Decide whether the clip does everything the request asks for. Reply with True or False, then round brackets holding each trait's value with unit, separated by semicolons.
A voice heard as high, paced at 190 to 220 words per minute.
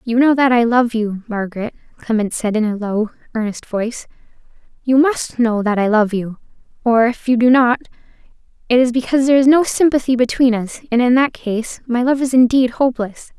True (240 Hz; 195 wpm)